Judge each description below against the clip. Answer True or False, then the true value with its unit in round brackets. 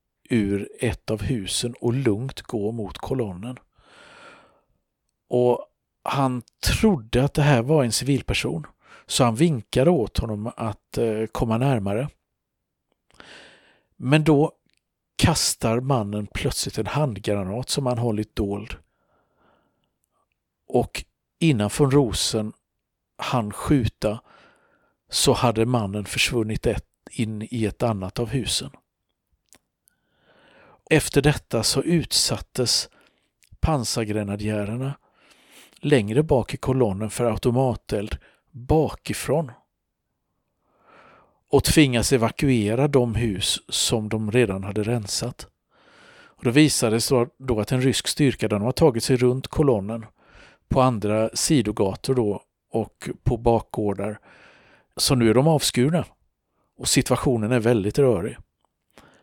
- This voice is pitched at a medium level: False (120 Hz)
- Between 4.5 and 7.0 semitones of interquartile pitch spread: False (3.7 semitones)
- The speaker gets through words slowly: True (105 wpm)